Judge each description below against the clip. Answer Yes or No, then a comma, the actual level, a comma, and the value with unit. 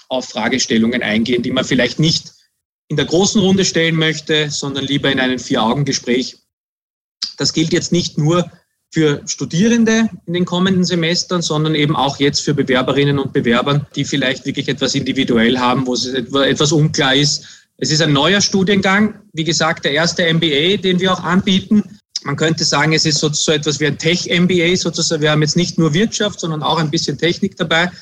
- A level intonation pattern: No, average, 4.0 semitones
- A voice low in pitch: No, medium, 155 Hz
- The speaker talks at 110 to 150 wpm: No, average, 180 wpm